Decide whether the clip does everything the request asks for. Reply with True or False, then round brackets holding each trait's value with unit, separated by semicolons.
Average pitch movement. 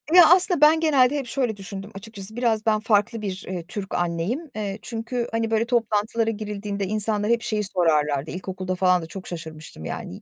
True (3.7 semitones)